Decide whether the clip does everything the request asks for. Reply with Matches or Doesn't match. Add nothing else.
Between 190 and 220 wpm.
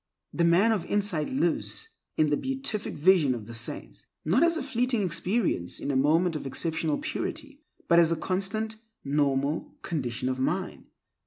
Doesn't match